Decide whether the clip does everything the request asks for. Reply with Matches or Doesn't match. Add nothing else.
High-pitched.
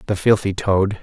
Doesn't match